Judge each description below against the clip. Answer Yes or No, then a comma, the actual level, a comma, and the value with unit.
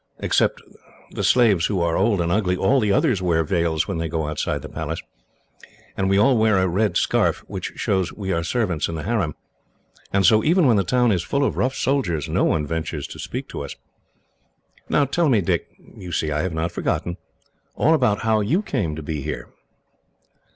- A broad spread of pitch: Yes, wide, 5.7 semitones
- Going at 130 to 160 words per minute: No, fast, 205 wpm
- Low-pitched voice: Yes, very low, 95 Hz